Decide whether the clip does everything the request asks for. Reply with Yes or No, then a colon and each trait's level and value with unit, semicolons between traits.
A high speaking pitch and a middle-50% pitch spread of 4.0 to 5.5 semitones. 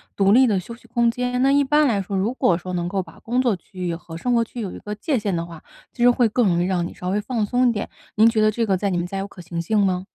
Yes: high, 210 Hz; average, 4.6 semitones